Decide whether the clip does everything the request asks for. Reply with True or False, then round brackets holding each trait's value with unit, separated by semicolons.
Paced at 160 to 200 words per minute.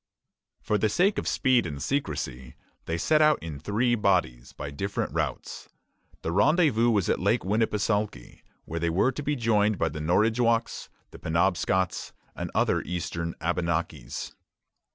False (145 wpm)